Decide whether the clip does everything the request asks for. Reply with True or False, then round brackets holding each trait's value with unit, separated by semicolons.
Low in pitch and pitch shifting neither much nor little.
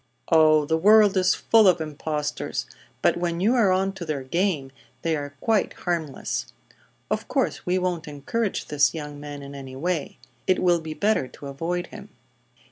False (165 Hz; 4.2 semitones)